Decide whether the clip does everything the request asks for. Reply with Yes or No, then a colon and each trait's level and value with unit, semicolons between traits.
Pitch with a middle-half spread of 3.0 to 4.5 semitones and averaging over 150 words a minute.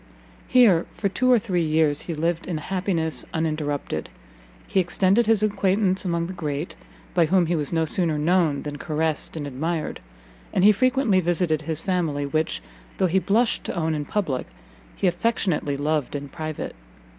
Yes: average, 3.6 semitones; average, 170 wpm